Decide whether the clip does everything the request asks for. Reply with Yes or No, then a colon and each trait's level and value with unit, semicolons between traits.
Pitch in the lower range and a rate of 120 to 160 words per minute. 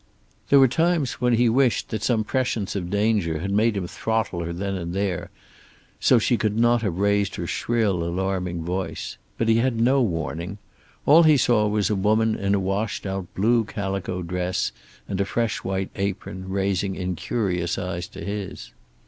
No: low, 100 Hz; average, 180 wpm